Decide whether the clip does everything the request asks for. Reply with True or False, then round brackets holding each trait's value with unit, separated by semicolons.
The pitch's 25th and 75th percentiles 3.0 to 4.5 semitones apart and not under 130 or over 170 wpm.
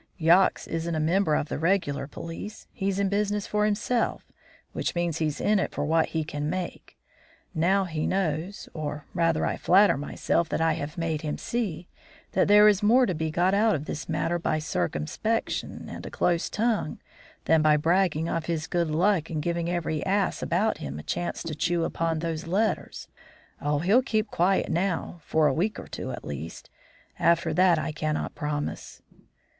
False (3.8 semitones; 185 wpm)